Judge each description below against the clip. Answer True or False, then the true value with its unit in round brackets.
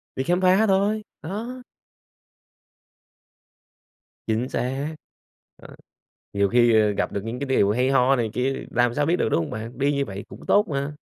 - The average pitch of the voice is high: False (130 Hz)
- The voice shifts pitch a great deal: True (6.2 semitones)